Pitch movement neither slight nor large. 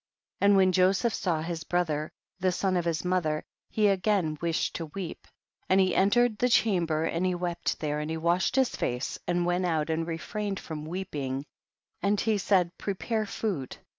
Yes: average, 3.5 semitones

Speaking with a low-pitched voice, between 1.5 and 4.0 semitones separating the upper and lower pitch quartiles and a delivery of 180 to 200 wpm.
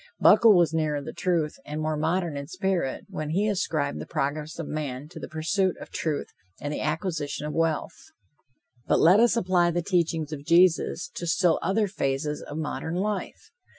No: medium, 165 Hz; average, 3.4 semitones; average, 185 wpm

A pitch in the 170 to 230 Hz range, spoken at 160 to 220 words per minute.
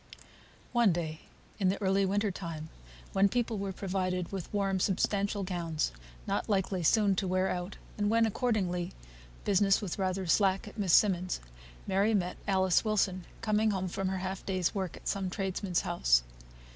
Yes: high, 190 Hz; average, 165 wpm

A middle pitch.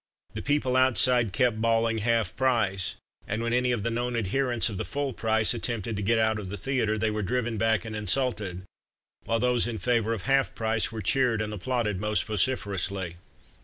No: low, 115 Hz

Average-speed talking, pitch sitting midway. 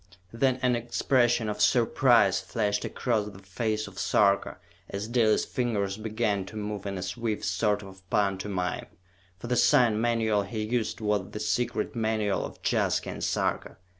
No: average, 160 wpm; low, 105 Hz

